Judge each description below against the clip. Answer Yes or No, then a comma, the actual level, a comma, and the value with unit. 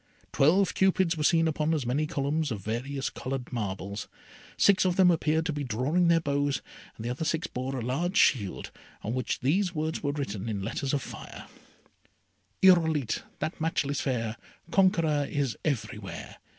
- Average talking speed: Yes, average, 165 wpm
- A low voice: No, medium, 145 Hz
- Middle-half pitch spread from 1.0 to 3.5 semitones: No, average, 4.6 semitones